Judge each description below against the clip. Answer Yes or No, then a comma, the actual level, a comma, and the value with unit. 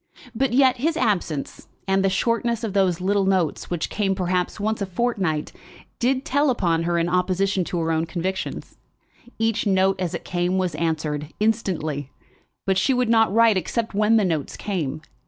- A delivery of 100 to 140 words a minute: No, average, 175 wpm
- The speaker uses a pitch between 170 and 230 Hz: Yes, high, 190 Hz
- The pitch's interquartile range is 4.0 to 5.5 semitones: Yes, average, 4.4 semitones